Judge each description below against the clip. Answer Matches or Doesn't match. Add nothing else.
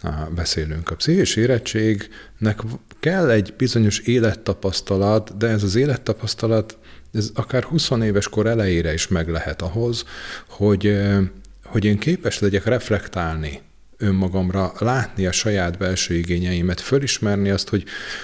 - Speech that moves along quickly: Doesn't match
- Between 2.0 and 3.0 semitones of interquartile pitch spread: Doesn't match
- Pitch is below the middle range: Matches